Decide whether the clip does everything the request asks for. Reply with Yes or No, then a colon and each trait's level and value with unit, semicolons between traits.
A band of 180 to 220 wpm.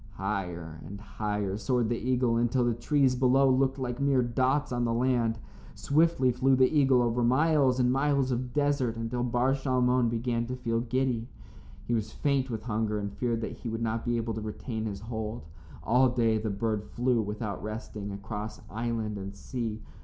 Yes: average, 185 wpm